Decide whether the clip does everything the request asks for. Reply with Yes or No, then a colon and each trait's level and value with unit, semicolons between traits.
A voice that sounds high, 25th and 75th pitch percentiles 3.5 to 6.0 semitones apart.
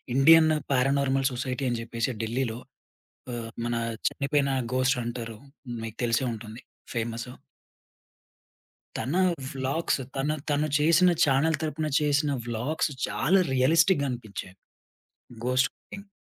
No: low, 135 Hz; average, 3.9 semitones